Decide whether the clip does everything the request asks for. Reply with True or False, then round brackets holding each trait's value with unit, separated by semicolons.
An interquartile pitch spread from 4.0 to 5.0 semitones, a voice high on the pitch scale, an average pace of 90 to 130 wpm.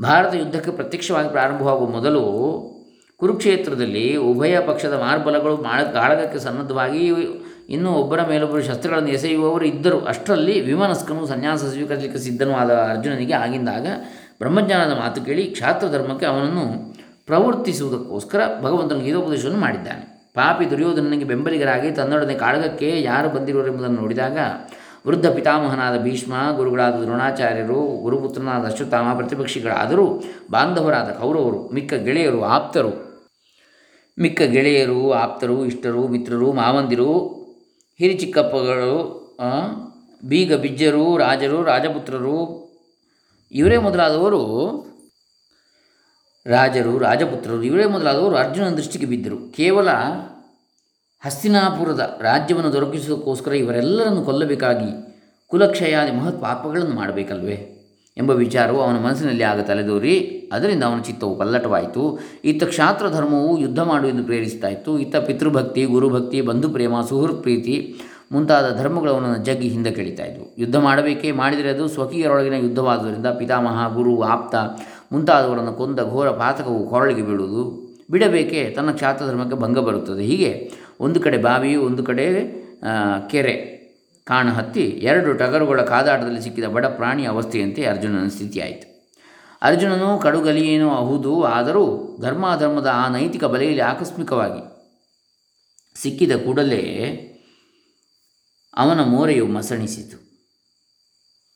False (4.4 semitones; 135 Hz; 100 wpm)